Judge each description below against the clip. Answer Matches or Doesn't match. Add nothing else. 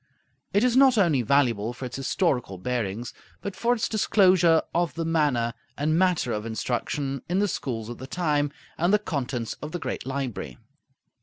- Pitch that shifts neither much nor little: Doesn't match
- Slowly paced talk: Doesn't match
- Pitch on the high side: Doesn't match